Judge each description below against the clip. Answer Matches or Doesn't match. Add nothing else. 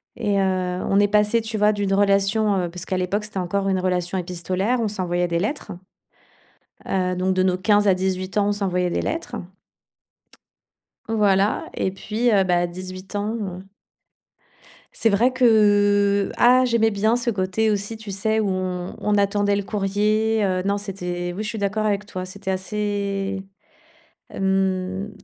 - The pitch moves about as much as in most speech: Doesn't match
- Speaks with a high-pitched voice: Matches